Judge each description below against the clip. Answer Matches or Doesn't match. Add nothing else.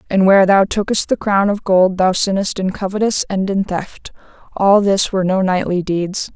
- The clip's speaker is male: Doesn't match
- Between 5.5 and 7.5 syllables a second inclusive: Doesn't match